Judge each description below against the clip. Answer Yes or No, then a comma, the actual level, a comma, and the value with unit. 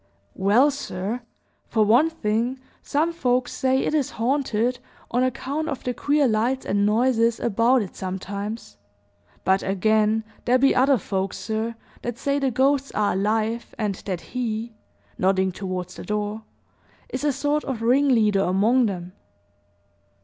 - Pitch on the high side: Yes, high, 230 Hz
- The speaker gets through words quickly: No, average, 145 wpm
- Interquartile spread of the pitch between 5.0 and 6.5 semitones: No, average, 4.0 semitones